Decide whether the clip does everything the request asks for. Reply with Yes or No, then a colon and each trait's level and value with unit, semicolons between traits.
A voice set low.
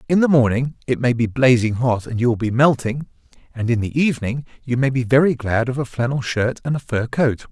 Yes: low, 125 Hz